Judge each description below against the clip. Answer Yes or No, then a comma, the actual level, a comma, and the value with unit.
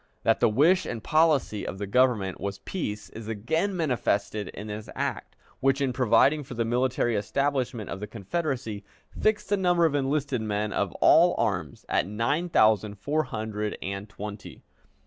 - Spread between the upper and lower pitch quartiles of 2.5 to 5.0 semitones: No, wide, 5.5 semitones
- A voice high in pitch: No, low, 115 Hz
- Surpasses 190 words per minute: No, average, 165 wpm